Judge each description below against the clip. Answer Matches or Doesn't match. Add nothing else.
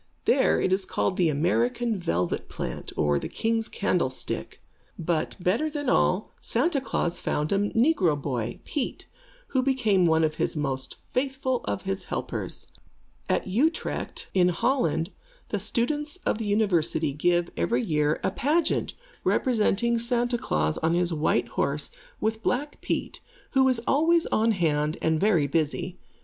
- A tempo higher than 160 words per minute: Doesn't match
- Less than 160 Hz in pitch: Doesn't match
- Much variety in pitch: Matches